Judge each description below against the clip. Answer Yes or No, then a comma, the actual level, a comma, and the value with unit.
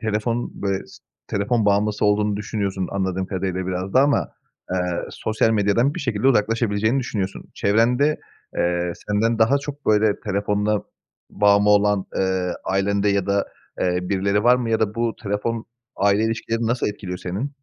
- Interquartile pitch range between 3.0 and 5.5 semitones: No, narrow, 2.5 semitones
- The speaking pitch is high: No, low, 105 Hz